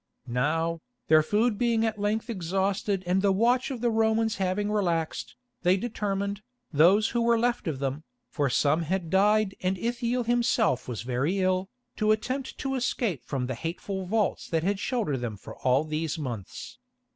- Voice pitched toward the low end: No, high, 195 Hz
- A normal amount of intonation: No, wide, 5.8 semitones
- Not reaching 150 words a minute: No, average, 170 wpm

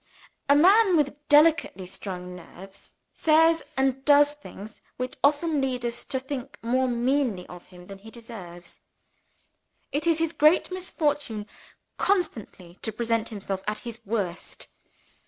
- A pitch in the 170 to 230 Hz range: No, very high, 250 Hz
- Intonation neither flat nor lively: No, wide, 6.6 semitones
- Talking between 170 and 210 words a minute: No, average, 140 wpm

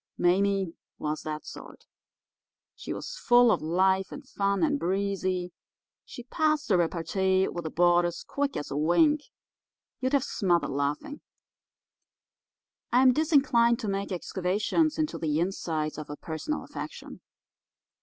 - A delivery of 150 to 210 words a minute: No, slow, 135 wpm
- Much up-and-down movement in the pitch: Yes, wide, 7.2 semitones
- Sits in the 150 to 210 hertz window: Yes, high, 190 Hz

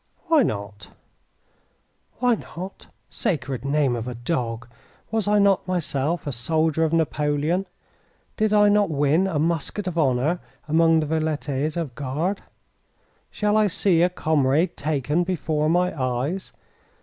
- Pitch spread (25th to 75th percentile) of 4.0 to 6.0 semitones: Yes, average, 4.4 semitones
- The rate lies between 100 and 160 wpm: Yes, average, 140 wpm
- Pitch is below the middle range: No, medium, 160 Hz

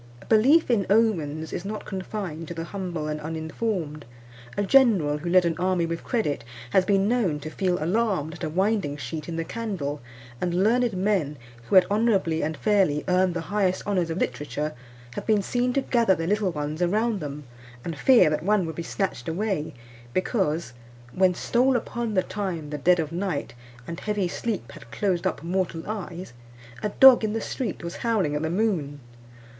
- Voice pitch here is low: No, medium, 185 Hz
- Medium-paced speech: Yes, average, 190 wpm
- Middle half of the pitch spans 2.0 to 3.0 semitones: No, average, 4.8 semitones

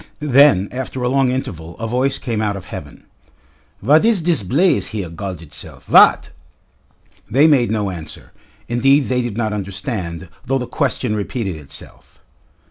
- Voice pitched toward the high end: No, low, 115 Hz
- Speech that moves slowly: No, average, 155 wpm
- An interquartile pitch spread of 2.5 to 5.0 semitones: No, wide, 5.6 semitones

